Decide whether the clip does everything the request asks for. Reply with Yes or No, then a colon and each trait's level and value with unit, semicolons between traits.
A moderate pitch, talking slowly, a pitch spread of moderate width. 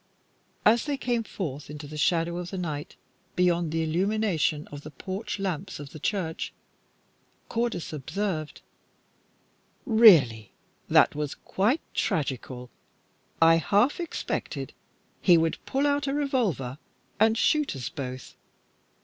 No: medium, 175 Hz; slow, 125 wpm; wide, 6.6 semitones